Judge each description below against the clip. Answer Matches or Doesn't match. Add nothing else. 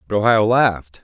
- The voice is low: Matches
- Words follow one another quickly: Doesn't match